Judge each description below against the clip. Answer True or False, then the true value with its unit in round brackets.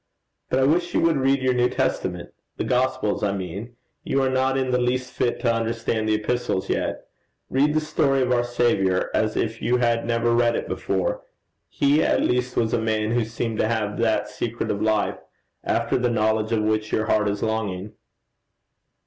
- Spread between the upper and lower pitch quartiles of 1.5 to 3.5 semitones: True (2.8 semitones)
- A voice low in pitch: True (120 Hz)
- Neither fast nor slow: True (195 wpm)